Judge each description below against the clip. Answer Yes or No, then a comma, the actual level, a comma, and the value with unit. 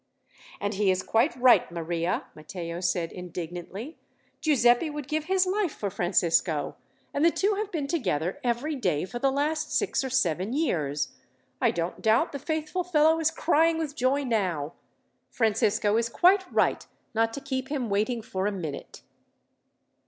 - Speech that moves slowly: No, average, 160 wpm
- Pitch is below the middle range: No, high, 235 Hz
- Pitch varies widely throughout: Yes, wide, 8.8 semitones